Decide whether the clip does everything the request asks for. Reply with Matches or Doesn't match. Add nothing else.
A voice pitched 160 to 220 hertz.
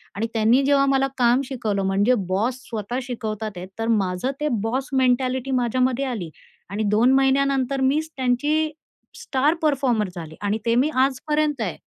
Doesn't match